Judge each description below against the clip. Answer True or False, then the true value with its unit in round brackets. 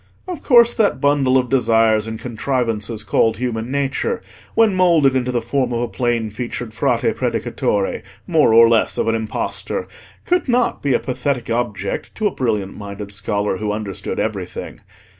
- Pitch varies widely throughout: False (4.3 semitones)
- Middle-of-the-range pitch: False (120 Hz)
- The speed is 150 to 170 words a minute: True (165 wpm)